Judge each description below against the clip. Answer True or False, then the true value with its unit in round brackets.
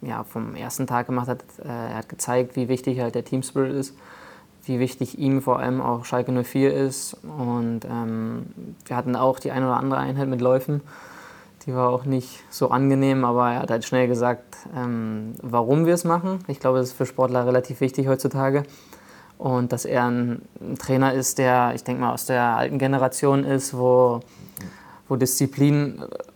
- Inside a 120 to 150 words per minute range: False (180 wpm)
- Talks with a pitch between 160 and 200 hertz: False (130 Hz)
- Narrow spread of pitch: True (1.8 semitones)